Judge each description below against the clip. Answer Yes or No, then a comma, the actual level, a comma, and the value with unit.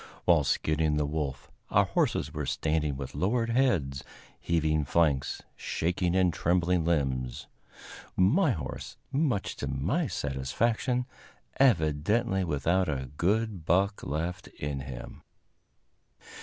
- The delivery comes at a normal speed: No, slow, 115 wpm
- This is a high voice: No, very low, 85 Hz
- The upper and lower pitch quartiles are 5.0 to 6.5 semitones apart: Yes, wide, 5.4 semitones